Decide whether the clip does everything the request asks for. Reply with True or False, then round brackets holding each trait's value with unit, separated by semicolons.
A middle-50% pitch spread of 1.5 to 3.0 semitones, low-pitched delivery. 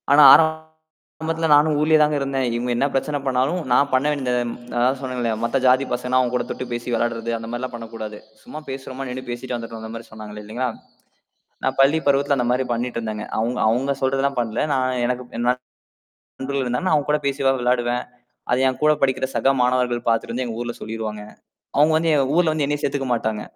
True (2.7 semitones; 130 Hz)